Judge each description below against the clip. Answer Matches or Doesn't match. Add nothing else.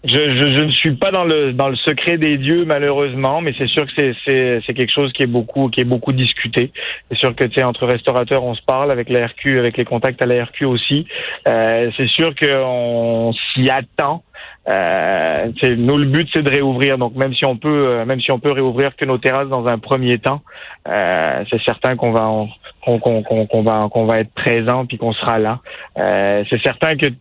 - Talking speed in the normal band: Doesn't match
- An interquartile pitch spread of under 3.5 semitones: Matches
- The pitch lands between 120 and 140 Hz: Matches